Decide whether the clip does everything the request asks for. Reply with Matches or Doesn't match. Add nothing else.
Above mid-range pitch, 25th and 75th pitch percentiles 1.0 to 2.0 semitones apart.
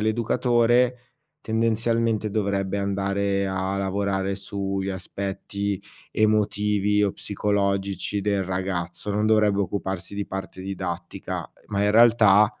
Doesn't match